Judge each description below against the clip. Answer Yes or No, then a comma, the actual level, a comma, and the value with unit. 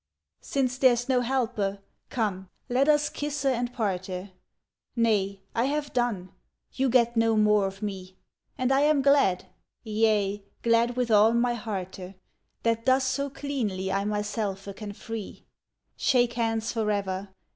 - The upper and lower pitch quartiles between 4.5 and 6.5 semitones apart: No, average, 4.1 semitones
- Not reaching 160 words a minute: Yes, average, 140 wpm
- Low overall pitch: No, high, 225 Hz